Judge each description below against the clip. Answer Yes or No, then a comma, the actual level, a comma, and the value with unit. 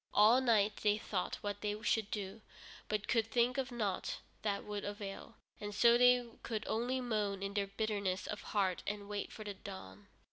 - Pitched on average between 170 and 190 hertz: No, high, 210 Hz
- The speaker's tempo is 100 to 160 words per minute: No, average, 185 wpm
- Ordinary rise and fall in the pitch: No, narrow, 2.0 semitones